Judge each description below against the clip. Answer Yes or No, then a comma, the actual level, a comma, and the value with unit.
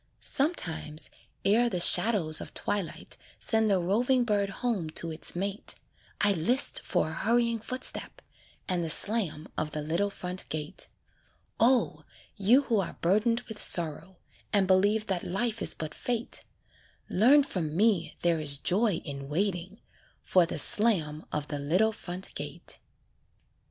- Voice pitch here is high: Yes, high, 195 Hz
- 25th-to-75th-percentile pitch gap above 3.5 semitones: Yes, average, 5.3 semitones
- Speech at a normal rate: Yes, average, 145 wpm